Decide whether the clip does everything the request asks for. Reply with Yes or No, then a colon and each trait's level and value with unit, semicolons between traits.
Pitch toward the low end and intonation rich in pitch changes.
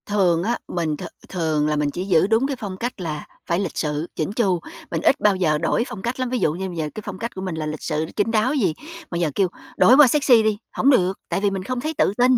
No: high, 190 Hz; wide, 6.1 semitones